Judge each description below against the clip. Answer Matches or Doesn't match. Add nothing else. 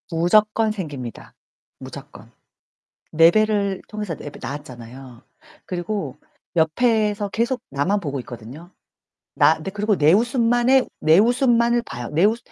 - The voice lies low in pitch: Doesn't match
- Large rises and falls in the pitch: Matches